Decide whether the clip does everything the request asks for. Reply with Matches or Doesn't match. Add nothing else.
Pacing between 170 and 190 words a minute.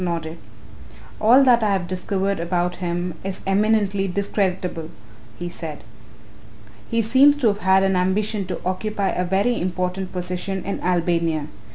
Doesn't match